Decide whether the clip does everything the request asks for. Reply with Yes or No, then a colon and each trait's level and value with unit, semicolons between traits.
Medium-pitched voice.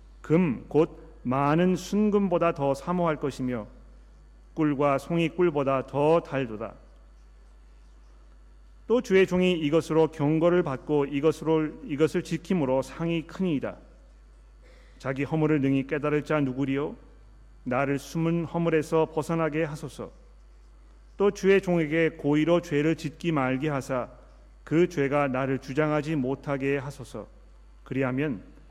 Yes: medium, 145 Hz